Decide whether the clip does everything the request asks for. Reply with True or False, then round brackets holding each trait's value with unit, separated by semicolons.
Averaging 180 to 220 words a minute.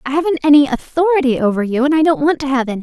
False (275 wpm)